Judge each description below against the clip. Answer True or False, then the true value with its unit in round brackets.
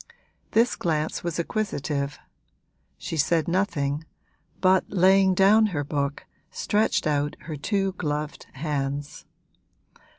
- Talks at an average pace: False (105 wpm)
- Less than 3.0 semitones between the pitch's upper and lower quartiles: False (4.7 semitones)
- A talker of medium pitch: True (160 Hz)